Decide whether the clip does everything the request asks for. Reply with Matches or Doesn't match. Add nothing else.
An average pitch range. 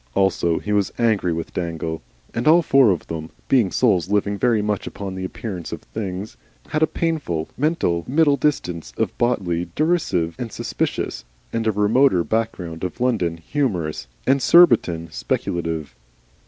Doesn't match